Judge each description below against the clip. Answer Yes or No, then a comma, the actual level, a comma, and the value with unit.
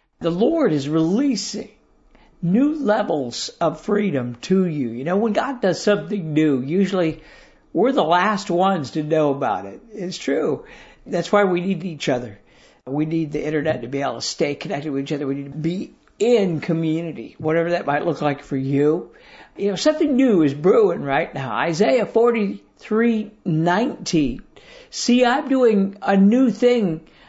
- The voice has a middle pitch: Yes, medium, 180 Hz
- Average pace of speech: Yes, average, 170 wpm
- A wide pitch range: Yes, wide, 5.9 semitones